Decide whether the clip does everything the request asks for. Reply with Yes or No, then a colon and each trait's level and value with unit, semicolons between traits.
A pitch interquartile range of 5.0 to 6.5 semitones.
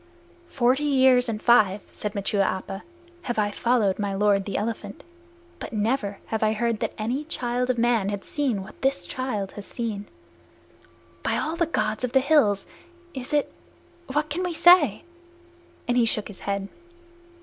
No: average, 4.3 semitones